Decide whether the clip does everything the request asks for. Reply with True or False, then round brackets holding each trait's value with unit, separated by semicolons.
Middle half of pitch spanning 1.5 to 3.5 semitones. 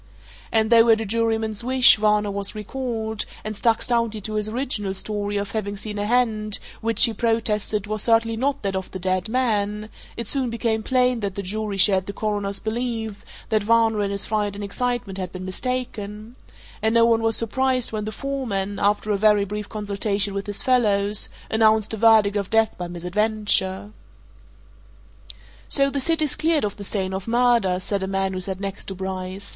True (2.4 semitones)